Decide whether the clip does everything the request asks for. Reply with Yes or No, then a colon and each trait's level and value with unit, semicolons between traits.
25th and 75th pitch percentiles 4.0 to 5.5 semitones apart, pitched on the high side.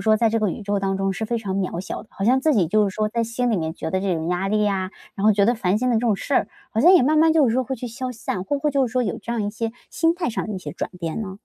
Yes: average, 4.3 semitones; high, 220 Hz